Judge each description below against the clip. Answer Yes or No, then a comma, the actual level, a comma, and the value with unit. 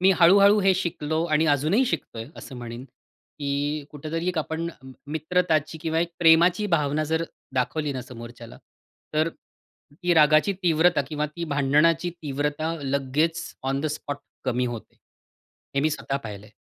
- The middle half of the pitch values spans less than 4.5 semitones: Yes, average, 3.1 semitones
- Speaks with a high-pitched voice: No, medium, 155 Hz